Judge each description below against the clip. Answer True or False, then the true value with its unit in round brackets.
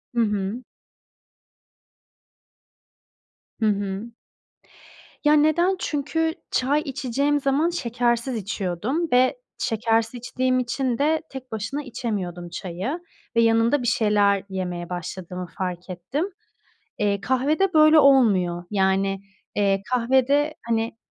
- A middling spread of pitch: False (6.1 semitones)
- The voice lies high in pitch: True (235 Hz)